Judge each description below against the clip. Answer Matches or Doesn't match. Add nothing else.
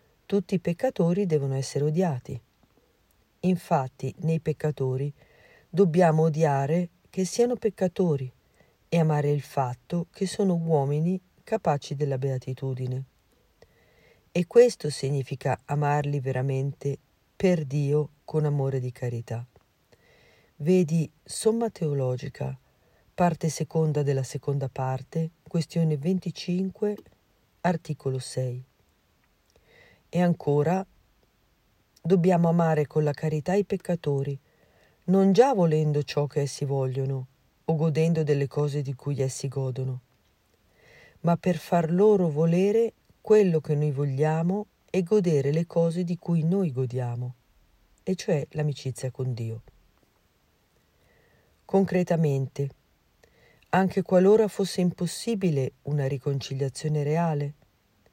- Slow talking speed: Matches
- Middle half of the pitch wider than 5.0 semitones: Doesn't match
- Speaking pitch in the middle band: Matches